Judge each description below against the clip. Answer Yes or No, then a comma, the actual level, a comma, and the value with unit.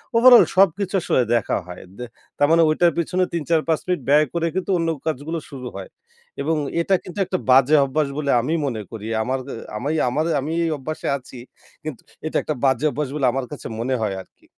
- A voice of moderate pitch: Yes, medium, 150 Hz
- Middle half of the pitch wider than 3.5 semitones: Yes, average, 4.2 semitones